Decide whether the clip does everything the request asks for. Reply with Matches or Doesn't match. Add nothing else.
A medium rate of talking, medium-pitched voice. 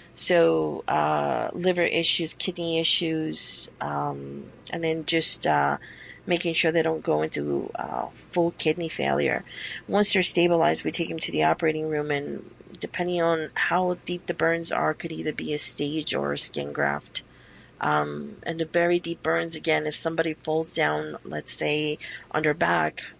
Matches